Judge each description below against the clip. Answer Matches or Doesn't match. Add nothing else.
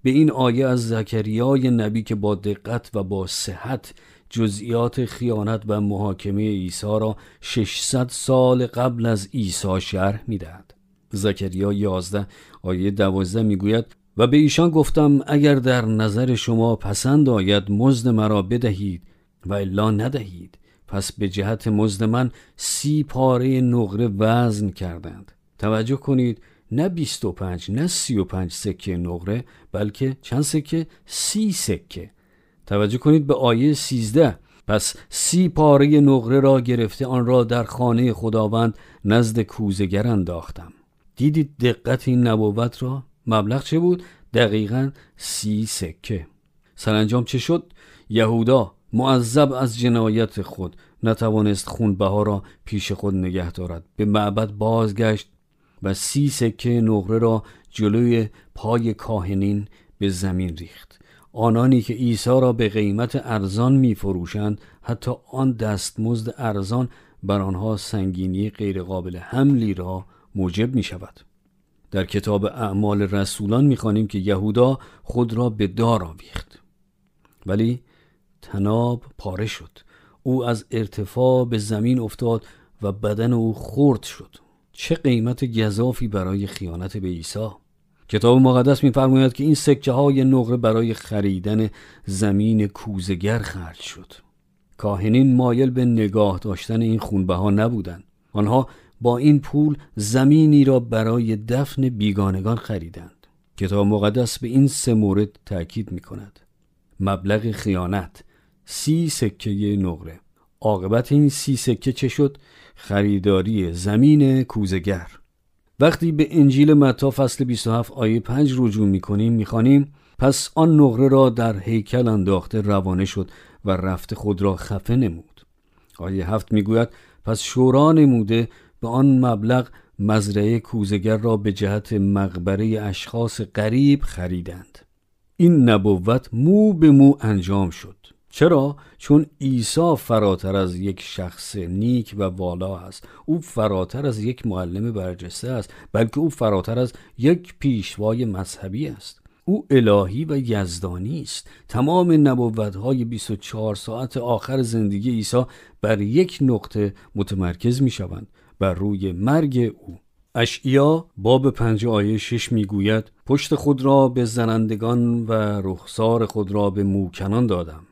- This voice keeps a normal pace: Matches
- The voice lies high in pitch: Doesn't match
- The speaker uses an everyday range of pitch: Matches